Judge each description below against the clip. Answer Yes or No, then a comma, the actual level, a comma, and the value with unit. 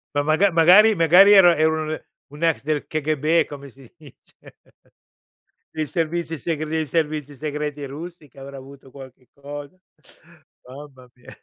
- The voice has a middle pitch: Yes, medium, 150 Hz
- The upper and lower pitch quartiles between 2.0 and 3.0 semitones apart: Yes, average, 2.7 semitones